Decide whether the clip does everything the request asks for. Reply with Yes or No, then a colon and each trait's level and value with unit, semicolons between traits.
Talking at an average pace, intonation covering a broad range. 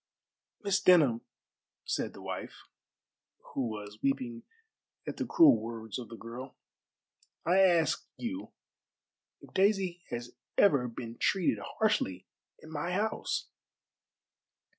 No: slow, 115 wpm; wide, 8.6 semitones